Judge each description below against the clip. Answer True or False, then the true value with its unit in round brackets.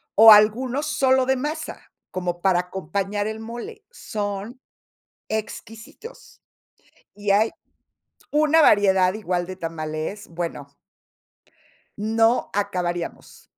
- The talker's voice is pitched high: True (210 Hz)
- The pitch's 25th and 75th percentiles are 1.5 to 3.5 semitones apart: False (4.9 semitones)